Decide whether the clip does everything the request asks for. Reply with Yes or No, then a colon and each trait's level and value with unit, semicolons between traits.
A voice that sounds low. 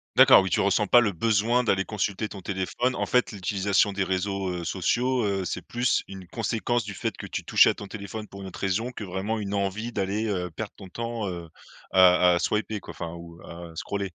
Yes: low, 100 Hz